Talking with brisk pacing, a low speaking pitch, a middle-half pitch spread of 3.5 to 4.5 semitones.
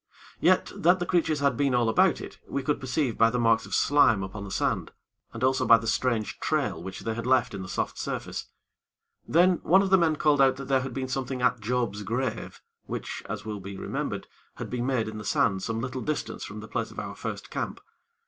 Yes: fast, 230 wpm; low, 125 Hz; average, 3.8 semitones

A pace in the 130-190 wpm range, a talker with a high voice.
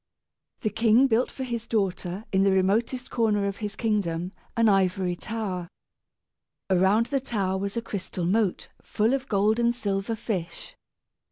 Yes: average, 155 wpm; high, 210 Hz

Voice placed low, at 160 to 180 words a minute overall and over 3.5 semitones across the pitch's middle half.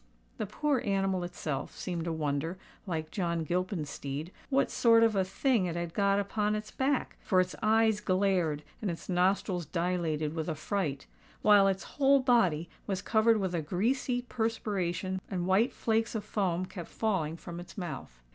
No: medium, 185 Hz; average, 170 wpm; average, 4.2 semitones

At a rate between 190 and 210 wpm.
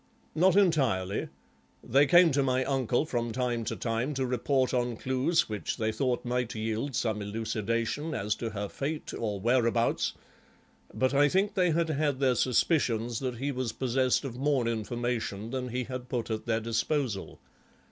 No: average, 165 wpm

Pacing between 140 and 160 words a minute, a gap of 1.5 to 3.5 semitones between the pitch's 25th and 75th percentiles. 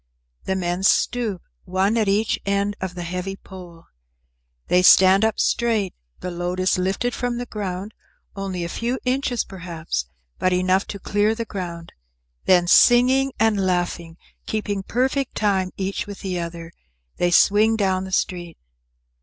Yes: average, 155 wpm; average, 3.2 semitones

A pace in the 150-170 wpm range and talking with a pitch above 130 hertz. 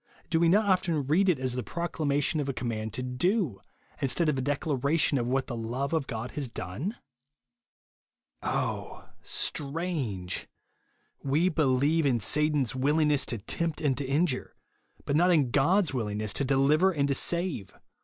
Yes: average, 165 wpm; medium, 140 Hz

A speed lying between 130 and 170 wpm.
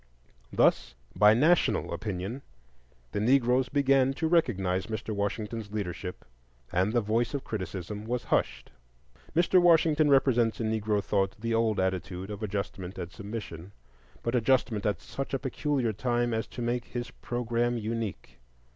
Yes: average, 145 wpm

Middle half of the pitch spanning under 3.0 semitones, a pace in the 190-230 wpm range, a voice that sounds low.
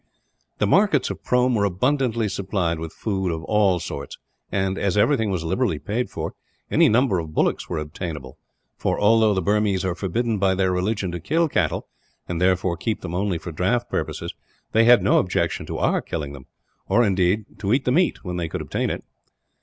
No: average, 4.2 semitones; average, 195 wpm; very low, 95 Hz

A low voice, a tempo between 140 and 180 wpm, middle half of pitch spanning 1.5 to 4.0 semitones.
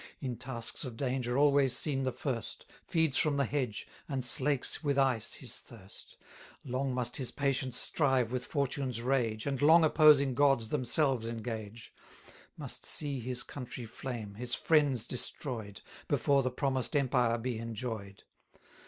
Yes: low, 130 Hz; average, 150 wpm; average, 3.0 semitones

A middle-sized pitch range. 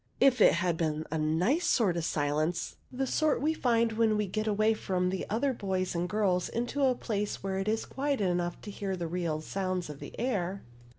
Yes: average, 4.7 semitones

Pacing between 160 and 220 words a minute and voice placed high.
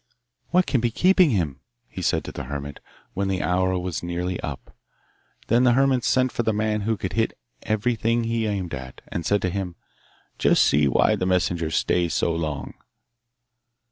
No: average, 180 wpm; very low, 95 Hz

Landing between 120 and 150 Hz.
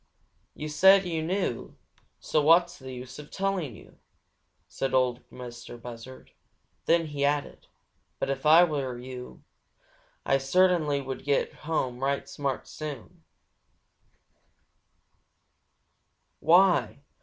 Yes: medium, 140 Hz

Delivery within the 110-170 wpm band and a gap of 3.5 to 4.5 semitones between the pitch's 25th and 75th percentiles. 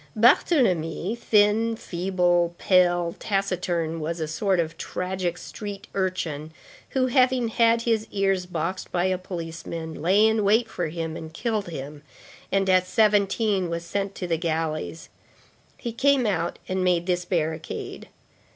Yes: average, 140 wpm; average, 3.8 semitones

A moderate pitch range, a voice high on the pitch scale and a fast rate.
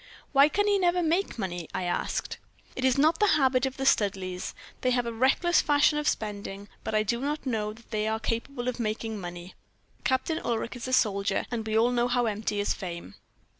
Yes: average, 4.5 semitones; high, 235 Hz; fast, 210 wpm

